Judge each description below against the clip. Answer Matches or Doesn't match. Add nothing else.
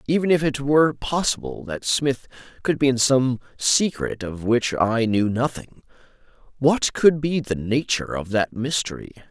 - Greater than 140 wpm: Matches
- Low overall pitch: Matches